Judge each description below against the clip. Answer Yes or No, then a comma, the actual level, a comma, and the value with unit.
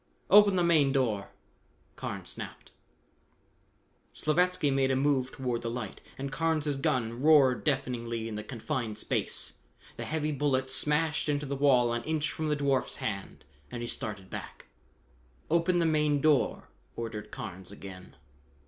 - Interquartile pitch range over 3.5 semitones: Yes, average, 4.5 semitones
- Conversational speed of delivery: Yes, average, 150 wpm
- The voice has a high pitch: No, low, 135 Hz